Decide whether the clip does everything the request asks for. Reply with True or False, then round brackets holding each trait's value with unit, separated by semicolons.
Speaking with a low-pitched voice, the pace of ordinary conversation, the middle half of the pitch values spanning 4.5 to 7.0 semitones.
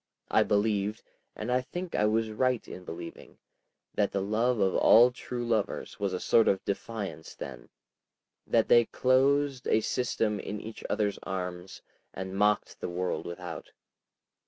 False (105 Hz; 155 wpm; 3.9 semitones)